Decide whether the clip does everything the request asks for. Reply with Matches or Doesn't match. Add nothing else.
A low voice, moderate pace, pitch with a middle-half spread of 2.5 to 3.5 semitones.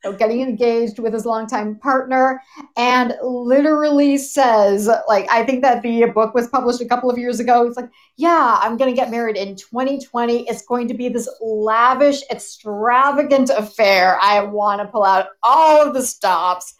Doesn't match